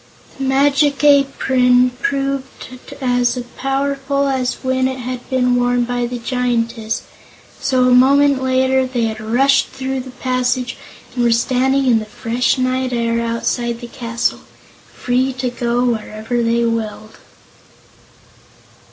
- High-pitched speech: Yes, very high, 250 Hz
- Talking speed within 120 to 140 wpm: Yes, slow, 135 wpm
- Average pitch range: No, narrow, 1.8 semitones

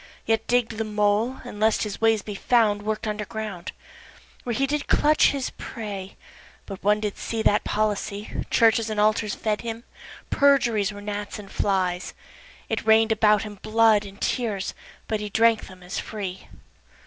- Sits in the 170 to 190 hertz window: No, high, 215 Hz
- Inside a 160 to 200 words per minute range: Yes, average, 170 wpm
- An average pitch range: No, narrow, 1.6 semitones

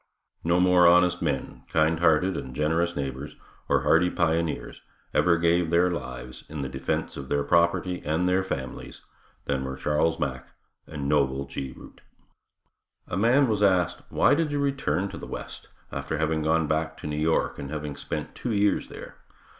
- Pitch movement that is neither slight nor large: Yes, average, 3.7 semitones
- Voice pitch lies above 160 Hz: No, very low, 80 Hz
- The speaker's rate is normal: Yes, average, 170 wpm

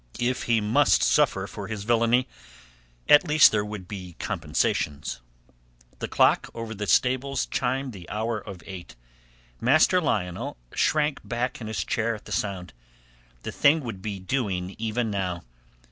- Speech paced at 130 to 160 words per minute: Yes, average, 150 wpm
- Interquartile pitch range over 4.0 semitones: Yes, average, 4.4 semitones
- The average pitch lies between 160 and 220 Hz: No, low, 110 Hz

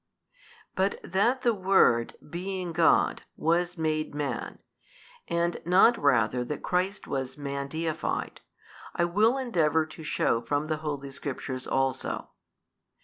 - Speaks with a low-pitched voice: No, medium, 160 Hz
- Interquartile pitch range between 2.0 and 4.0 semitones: No, average, 4.5 semitones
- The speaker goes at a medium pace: No, slow, 125 wpm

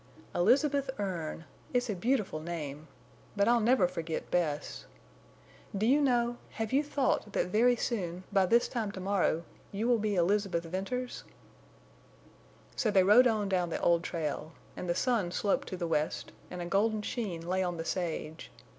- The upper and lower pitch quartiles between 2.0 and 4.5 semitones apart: No, average, 5.3 semitones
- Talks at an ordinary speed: Yes, average, 160 wpm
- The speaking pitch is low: No, high, 195 Hz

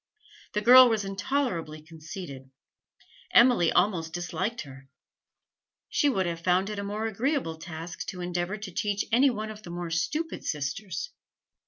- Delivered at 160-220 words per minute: No, average, 150 wpm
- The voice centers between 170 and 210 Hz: Yes, high, 190 Hz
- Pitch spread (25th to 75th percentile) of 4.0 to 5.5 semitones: Yes, average, 4.8 semitones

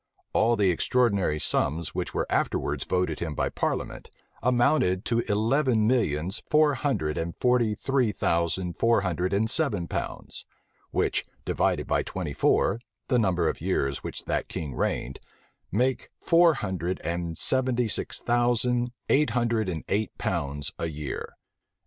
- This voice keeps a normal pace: Yes, average, 150 wpm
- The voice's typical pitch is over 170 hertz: No, low, 105 Hz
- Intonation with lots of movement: Yes, wide, 6.4 semitones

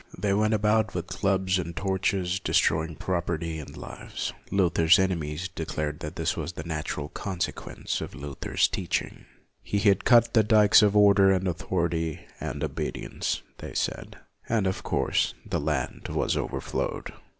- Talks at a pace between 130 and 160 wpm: Yes, average, 150 wpm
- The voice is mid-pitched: No, very low, 90 Hz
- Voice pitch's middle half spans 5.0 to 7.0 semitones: No, average, 3.6 semitones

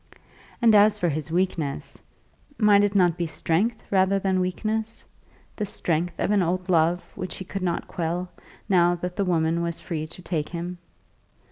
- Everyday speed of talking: Yes, average, 170 wpm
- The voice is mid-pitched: Yes, medium, 180 Hz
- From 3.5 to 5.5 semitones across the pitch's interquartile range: No, average, 2.7 semitones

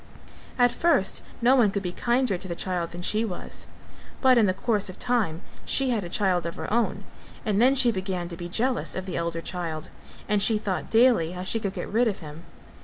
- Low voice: No, high, 195 Hz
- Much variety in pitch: No, average, 5.0 semitones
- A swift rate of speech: Yes, fast, 225 wpm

